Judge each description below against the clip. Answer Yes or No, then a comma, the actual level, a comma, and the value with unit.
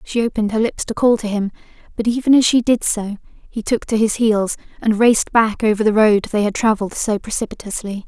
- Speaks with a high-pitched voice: Yes, high, 215 Hz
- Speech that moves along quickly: Yes, fast, 225 wpm